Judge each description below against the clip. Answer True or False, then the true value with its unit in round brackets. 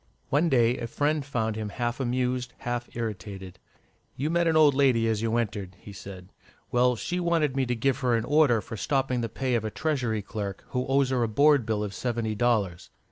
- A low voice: True (120 Hz)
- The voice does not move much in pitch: False (3.6 semitones)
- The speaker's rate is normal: False (210 wpm)